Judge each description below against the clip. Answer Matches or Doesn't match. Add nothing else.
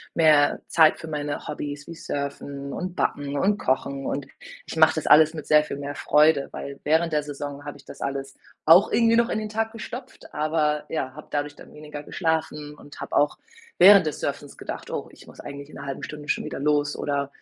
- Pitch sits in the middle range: Matches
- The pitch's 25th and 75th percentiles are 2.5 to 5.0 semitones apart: Doesn't match